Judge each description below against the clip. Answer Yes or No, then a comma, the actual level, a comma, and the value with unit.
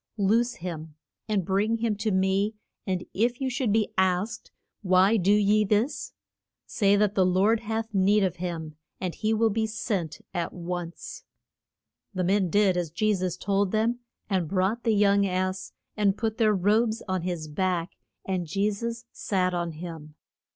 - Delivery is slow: No, average, 170 wpm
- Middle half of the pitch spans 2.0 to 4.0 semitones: Yes, average, 2.9 semitones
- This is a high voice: Yes, high, 195 Hz